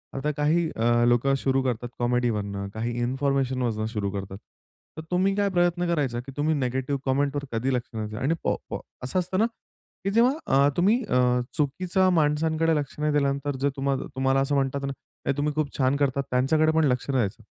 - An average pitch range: Yes, average, 3.9 semitones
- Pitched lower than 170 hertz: Yes, medium, 140 Hz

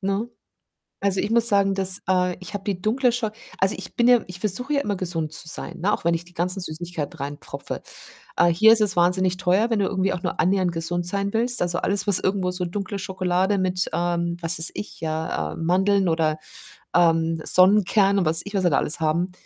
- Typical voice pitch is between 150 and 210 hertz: Yes, medium, 185 Hz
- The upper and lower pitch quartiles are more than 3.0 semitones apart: No, average, 2.7 semitones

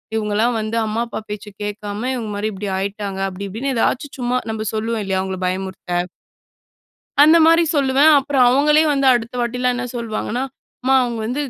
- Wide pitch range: No, average, 3.7 semitones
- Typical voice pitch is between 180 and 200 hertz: No, high, 230 Hz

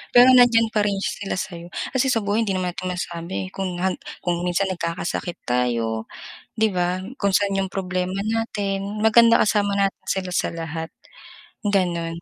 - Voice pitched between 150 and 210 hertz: Yes, high, 190 Hz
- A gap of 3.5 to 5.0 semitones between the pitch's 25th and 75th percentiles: No, average, 2.9 semitones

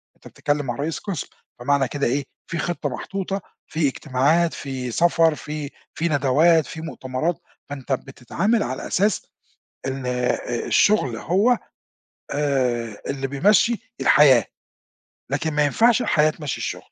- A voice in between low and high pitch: Yes, medium, 145 Hz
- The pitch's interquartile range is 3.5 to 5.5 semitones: Yes, average, 4.3 semitones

